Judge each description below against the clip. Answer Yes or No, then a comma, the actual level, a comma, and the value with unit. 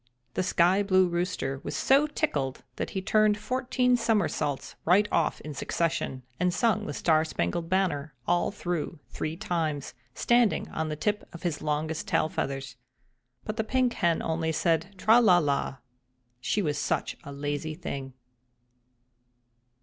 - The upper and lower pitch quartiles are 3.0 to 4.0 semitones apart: No, wide, 5.6 semitones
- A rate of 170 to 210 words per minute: No, average, 150 wpm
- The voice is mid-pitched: Yes, medium, 170 Hz